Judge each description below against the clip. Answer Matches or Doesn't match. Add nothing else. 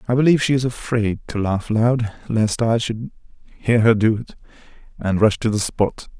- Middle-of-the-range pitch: Doesn't match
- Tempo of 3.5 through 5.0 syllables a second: Matches